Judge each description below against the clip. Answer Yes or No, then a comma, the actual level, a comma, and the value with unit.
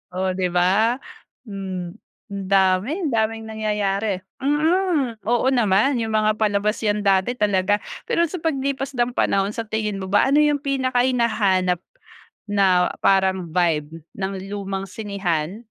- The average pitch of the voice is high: Yes, high, 210 Hz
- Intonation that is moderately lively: Yes, average, 4.2 semitones